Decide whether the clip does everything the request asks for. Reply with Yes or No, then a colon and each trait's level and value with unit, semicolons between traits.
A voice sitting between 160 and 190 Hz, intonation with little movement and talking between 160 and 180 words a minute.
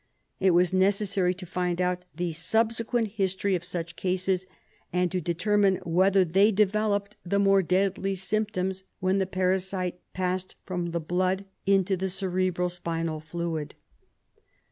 No: medium, 185 Hz; narrow, 1.7 semitones; average, 140 wpm